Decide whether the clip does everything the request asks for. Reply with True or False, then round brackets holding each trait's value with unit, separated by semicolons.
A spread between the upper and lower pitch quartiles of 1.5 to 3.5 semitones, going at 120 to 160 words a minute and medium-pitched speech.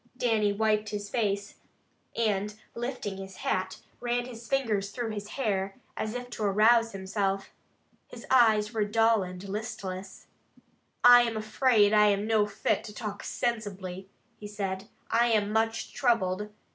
False (2.5 semitones; 145 wpm; 210 Hz)